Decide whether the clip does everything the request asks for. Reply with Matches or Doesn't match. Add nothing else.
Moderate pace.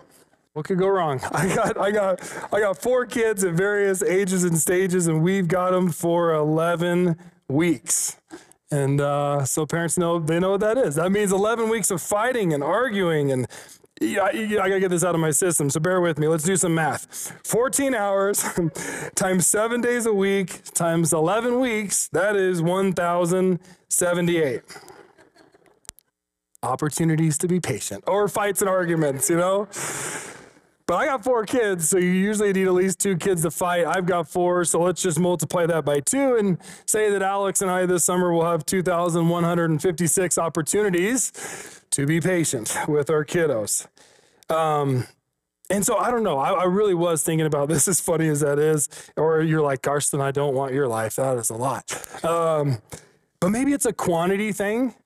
Matches